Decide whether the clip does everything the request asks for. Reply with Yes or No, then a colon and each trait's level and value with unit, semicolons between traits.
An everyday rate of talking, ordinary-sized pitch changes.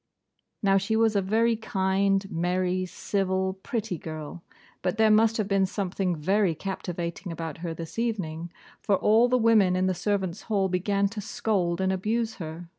Yes: average, 170 wpm; average, 3.2 semitones